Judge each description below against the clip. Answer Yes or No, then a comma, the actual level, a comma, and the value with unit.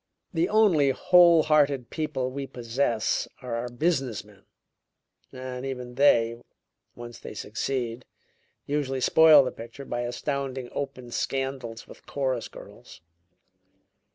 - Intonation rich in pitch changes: No, average, 2.8 semitones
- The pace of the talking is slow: Yes, slow, 120 wpm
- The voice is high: No, low, 130 Hz